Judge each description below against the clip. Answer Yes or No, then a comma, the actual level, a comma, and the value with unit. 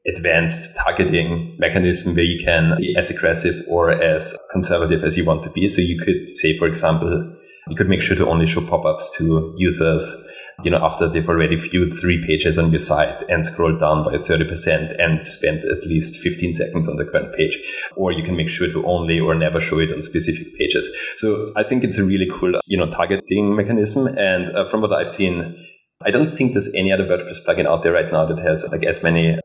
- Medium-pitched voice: No, very low, 85 Hz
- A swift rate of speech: Yes, fast, 220 wpm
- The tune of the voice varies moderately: Yes, average, 3.0 semitones